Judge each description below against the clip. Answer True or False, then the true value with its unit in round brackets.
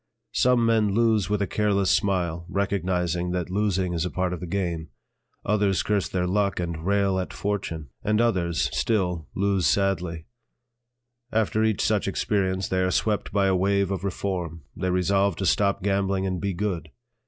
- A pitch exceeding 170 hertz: False (95 Hz)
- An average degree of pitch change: False (2.1 semitones)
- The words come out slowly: False (170 wpm)